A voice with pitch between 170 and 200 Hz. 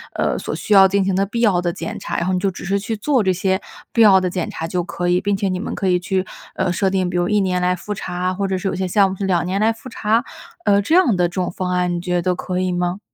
Yes: high, 190 Hz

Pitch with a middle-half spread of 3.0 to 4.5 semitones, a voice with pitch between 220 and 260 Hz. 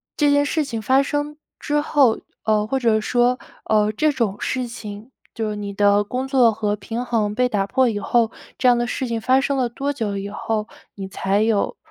Yes: average, 3.9 semitones; high, 230 Hz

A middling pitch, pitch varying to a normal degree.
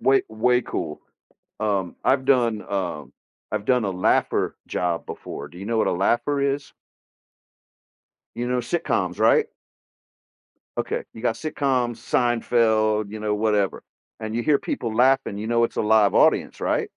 No: low, 115 Hz; average, 3.3 semitones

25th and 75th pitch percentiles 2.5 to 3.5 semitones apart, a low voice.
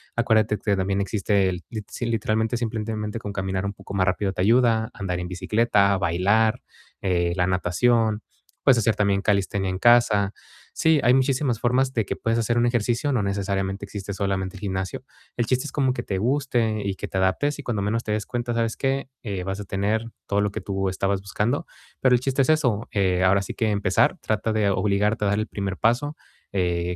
Yes: average, 3.2 semitones; low, 105 Hz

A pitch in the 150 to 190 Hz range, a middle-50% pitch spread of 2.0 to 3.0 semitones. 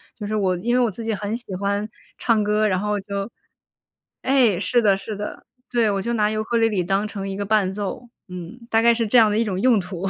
No: high, 210 Hz; narrow, 2.5 semitones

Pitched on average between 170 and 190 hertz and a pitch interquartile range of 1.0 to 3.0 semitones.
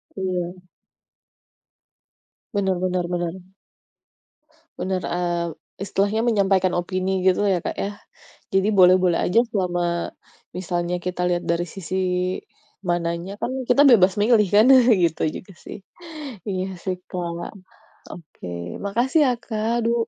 Yes: medium, 185 Hz; narrow, 2.4 semitones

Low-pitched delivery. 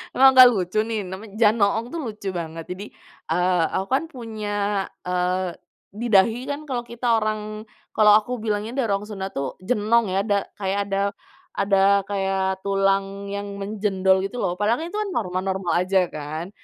No: high, 200 Hz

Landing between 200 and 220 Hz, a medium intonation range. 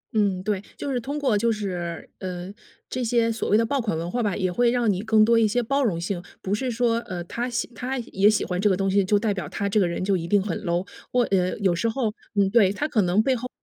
Yes: high, 210 Hz; average, 3.9 semitones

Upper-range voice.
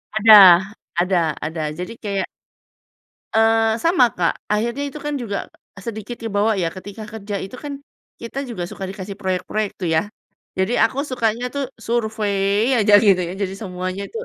Yes: high, 210 Hz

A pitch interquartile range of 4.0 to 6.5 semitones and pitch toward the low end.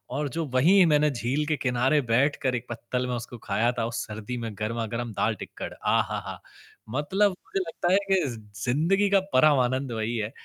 Yes: average, 4.6 semitones; low, 130 Hz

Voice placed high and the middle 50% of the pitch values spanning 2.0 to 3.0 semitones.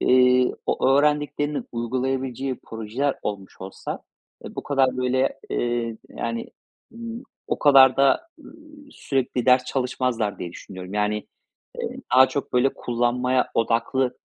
No: low, 125 Hz; narrow, 2.4 semitones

